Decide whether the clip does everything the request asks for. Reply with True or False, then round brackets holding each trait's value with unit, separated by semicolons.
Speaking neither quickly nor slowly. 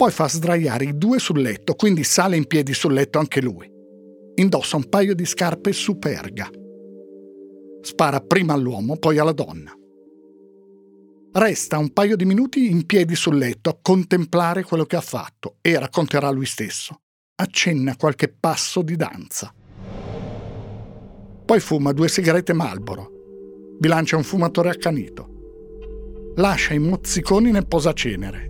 True (135 wpm)